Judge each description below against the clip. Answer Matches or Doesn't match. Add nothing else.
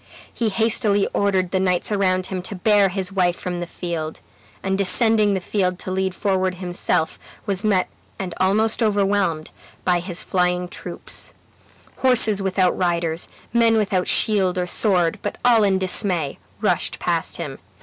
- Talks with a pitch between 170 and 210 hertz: Matches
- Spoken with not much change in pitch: Matches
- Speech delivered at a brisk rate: Doesn't match